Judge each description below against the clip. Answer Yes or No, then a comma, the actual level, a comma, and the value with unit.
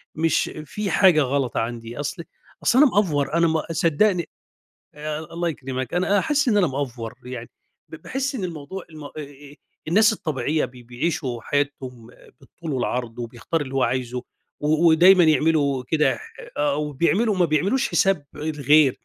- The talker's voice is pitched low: No, medium, 150 Hz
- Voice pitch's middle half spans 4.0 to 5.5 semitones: Yes, average, 5.0 semitones